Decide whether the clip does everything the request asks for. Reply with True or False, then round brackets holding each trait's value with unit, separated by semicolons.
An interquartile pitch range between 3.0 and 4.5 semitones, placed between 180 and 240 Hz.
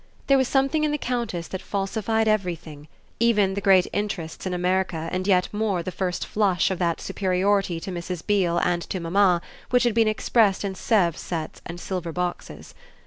True (3.3 semitones; 190 Hz)